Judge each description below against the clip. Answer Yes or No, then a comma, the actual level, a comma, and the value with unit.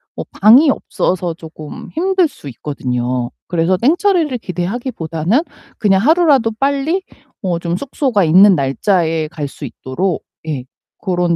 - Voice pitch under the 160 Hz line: No, medium, 185 Hz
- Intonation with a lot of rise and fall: Yes, wide, 8.7 semitones